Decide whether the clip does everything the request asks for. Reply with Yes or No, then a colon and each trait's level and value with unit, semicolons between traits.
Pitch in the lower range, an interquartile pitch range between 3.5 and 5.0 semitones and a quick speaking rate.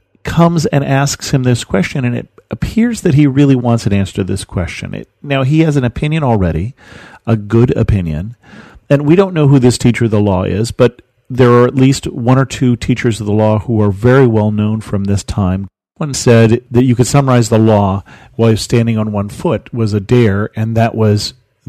Yes: low, 120 Hz; average, 4.2 semitones; fast, 215 wpm